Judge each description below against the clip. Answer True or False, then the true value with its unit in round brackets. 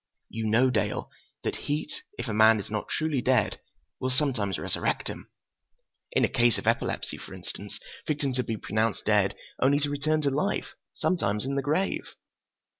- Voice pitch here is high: False (130 Hz)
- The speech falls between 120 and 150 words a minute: False (170 wpm)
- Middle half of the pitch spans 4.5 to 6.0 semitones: True (4.8 semitones)